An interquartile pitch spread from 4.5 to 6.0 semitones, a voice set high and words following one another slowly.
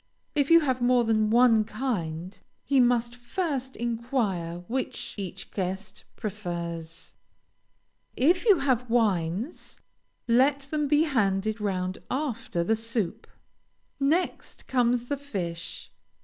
Yes: average, 5.3 semitones; high, 235 Hz; slow, 115 wpm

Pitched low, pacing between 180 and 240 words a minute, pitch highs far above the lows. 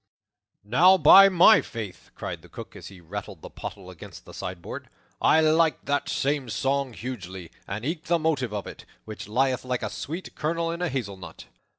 Yes: low, 130 Hz; average, 185 wpm; wide, 7.9 semitones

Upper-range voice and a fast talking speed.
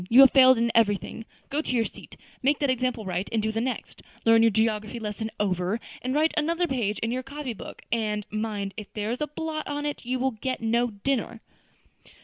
Yes: high, 230 Hz; fast, 215 wpm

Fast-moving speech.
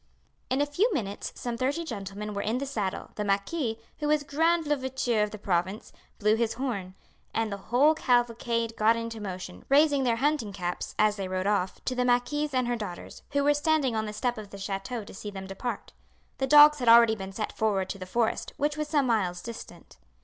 Yes: fast, 215 wpm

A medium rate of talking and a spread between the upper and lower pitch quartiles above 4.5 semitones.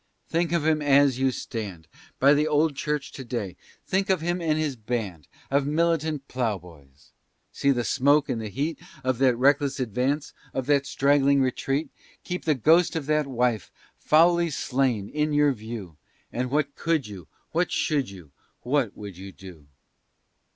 Yes: average, 165 wpm; average, 4.9 semitones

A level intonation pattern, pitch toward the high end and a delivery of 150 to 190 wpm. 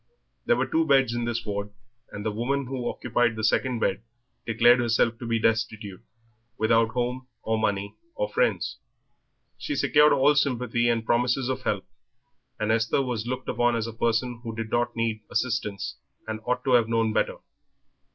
No: narrow, 2.1 semitones; low, 120 Hz; average, 175 wpm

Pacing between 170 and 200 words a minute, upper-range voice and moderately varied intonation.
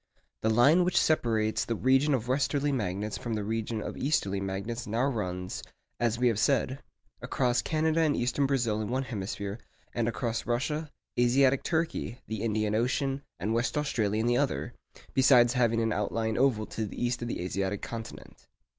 No: average, 175 wpm; low, 120 Hz; average, 3.7 semitones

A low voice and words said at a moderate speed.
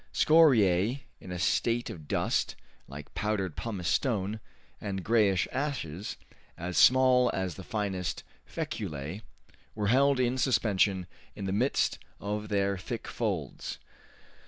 No: low, 105 Hz; slow, 125 wpm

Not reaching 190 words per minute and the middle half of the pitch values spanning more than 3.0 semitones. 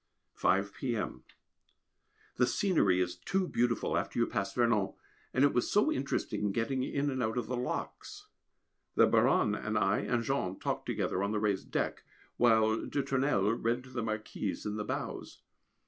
Yes: average, 170 wpm; average, 3.8 semitones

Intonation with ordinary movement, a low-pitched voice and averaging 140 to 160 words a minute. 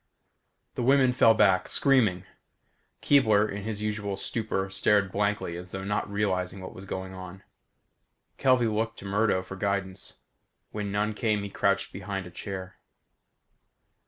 No: narrow, 2.1 semitones; low, 100 Hz; average, 145 wpm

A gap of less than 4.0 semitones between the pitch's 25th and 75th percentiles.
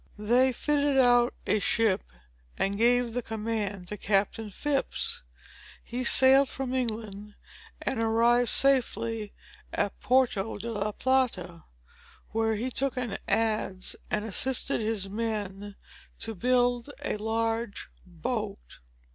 Yes: average, 3.0 semitones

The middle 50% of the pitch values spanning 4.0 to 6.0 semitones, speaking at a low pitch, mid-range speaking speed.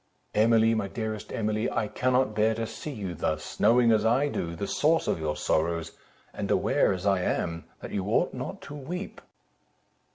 Yes: average, 4.3 semitones; low, 110 Hz; average, 185 wpm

